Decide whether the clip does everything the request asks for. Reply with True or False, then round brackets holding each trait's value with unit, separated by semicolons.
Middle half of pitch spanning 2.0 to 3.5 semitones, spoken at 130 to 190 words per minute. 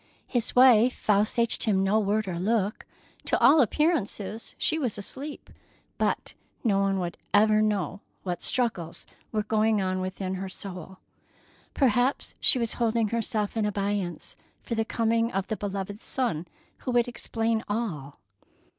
True (3.1 semitones; 145 wpm)